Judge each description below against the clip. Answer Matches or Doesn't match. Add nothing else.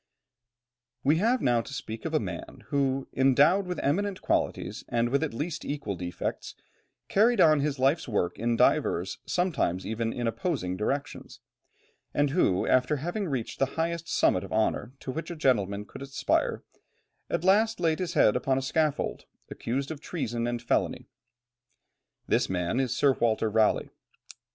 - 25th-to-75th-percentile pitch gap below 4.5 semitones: Doesn't match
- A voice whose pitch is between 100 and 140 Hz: Matches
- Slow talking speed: Doesn't match